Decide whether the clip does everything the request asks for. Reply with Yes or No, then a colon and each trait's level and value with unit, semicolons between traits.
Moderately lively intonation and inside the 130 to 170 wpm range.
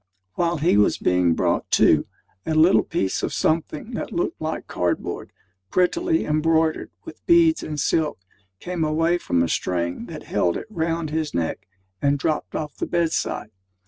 Yes: average, 3.4 semitones; average, 165 wpm